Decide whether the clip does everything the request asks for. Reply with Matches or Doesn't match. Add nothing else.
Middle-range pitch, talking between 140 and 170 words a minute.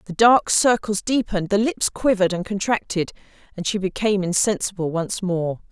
Doesn't match